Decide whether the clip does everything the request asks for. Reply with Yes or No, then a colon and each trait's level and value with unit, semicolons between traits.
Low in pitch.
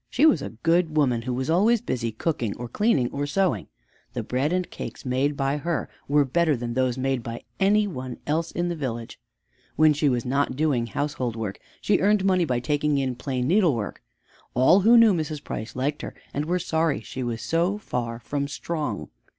No: medium, 145 Hz